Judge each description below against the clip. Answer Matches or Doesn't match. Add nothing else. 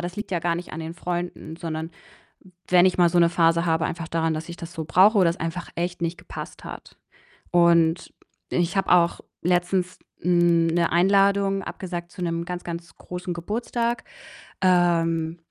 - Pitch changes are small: Matches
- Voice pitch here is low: Doesn't match